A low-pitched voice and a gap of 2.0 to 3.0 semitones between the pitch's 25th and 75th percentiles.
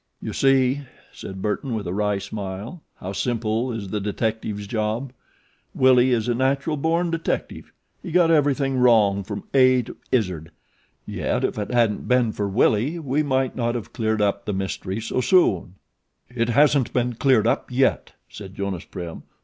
No: low, 115 Hz; average, 4.3 semitones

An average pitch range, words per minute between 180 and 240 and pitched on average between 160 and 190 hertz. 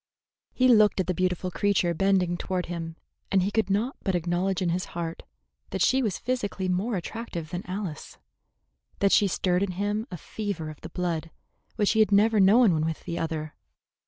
Yes: average, 3.0 semitones; average, 190 wpm; medium, 185 Hz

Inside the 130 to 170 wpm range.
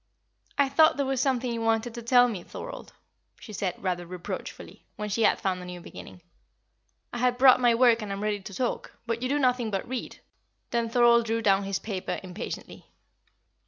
No: average, 195 wpm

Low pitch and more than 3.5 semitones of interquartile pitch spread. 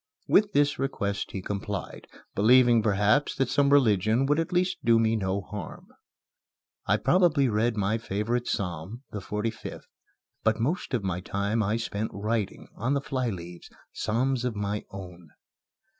Yes: low, 110 Hz; average, 4.4 semitones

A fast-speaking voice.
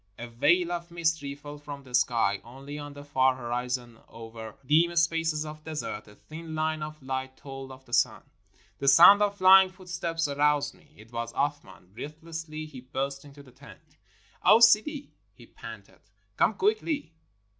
No: average, 165 wpm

